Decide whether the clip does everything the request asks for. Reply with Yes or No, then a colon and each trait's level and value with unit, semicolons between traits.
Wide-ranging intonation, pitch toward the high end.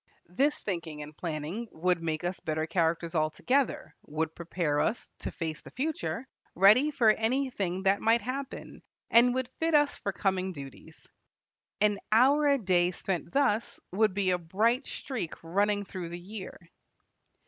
Yes: wide, 6.0 semitones; high, 195 Hz